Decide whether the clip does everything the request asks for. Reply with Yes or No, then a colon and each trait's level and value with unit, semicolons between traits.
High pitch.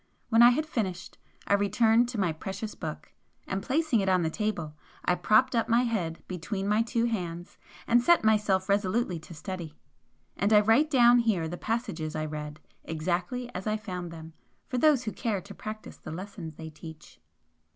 Yes: high, 200 Hz